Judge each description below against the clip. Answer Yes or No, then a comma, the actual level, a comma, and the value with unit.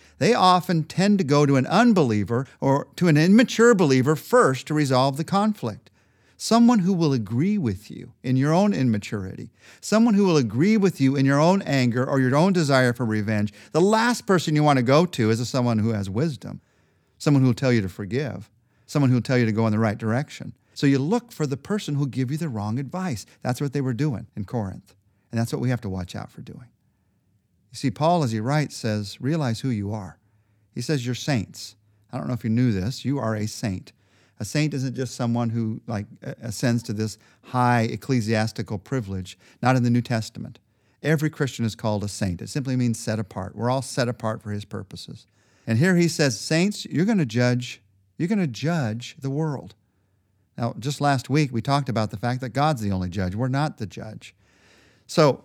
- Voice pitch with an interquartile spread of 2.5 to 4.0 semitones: No, wide, 5.4 semitones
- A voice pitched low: Yes, low, 125 Hz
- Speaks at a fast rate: Yes, fast, 215 wpm